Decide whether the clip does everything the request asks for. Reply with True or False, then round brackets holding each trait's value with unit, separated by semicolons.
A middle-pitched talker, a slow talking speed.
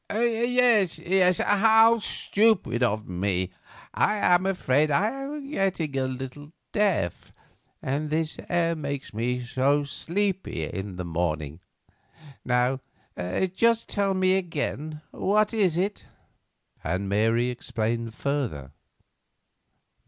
True (150 Hz; 110 wpm)